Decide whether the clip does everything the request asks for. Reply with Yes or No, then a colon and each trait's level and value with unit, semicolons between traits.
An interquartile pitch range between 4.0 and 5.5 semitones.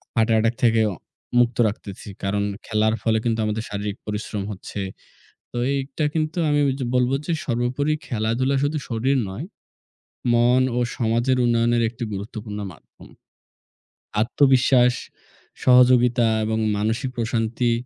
No: narrow, 2.6 semitones